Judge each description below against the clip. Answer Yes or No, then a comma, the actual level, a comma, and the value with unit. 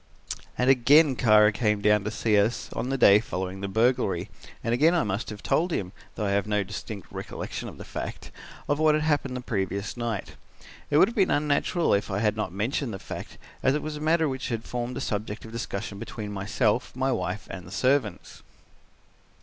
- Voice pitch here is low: Yes, low, 110 Hz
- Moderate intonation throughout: Yes, average, 4.8 semitones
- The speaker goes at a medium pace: No, fast, 210 wpm